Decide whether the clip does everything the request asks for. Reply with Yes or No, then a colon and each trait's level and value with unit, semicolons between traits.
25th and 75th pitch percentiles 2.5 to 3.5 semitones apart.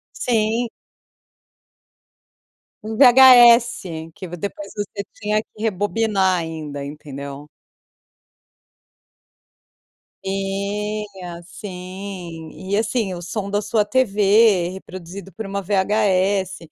Yes: average, 3.0 semitones